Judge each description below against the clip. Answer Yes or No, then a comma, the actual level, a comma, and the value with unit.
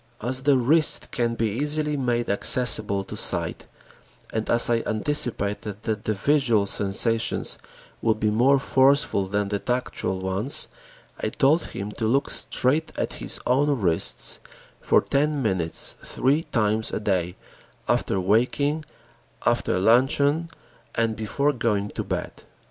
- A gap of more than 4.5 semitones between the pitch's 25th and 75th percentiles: Yes, average, 5.1 semitones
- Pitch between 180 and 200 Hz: No, low, 115 Hz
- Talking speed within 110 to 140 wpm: Yes, slow, 135 wpm